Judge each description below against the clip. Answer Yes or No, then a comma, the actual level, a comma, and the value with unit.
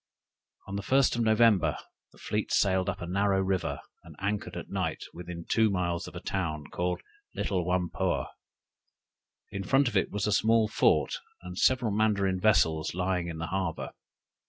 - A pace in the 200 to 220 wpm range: No, average, 170 wpm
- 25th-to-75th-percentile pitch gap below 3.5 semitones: Yes, average, 3.1 semitones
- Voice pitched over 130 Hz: No, very low, 95 Hz